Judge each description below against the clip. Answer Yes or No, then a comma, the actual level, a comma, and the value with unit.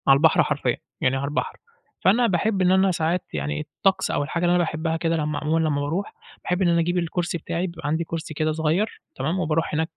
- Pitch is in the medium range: Yes, medium, 165 Hz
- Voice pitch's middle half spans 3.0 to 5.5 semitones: No, narrow, 2.6 semitones